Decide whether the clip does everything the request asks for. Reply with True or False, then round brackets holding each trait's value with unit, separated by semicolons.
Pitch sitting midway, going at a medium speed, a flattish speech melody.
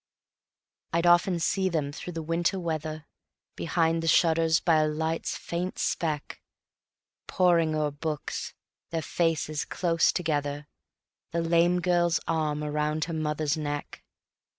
False (160 Hz; 130 wpm; 1.9 semitones)